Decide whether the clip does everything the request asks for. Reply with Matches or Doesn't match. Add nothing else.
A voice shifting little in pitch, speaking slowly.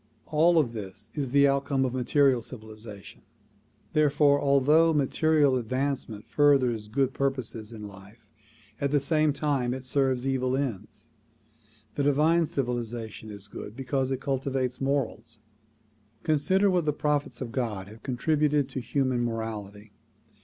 Doesn't match